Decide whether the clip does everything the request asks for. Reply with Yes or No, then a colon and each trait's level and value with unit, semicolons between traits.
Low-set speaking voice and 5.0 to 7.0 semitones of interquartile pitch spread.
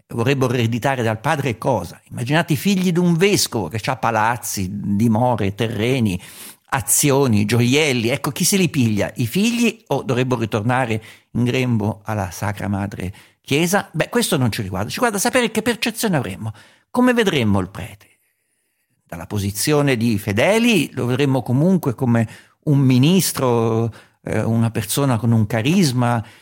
Yes: low, 120 Hz; wide, 5.6 semitones